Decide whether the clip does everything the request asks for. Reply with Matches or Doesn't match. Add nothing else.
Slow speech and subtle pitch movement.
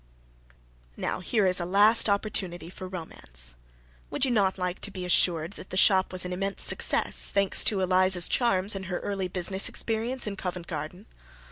Doesn't match